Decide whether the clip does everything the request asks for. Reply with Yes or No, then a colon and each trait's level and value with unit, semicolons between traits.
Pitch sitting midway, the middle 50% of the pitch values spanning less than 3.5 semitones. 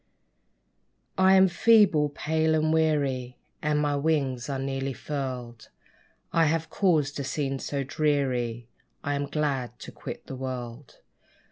Yes: medium, 145 Hz; average, 3.1 semitones